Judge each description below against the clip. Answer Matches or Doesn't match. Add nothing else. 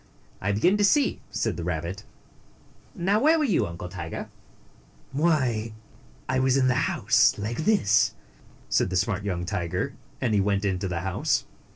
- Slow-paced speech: Doesn't match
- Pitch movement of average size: Doesn't match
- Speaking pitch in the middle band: Doesn't match